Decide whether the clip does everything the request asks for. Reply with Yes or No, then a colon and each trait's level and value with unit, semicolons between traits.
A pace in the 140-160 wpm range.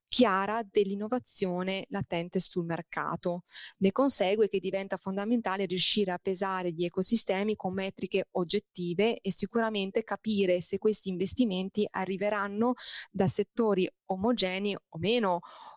No: slow, 115 wpm